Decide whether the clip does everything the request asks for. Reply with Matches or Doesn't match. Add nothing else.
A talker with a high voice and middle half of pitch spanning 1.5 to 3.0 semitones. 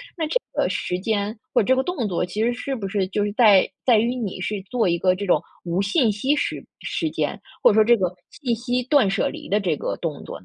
Doesn't match